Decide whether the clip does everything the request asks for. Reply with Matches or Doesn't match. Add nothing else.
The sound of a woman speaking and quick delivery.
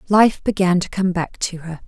Matches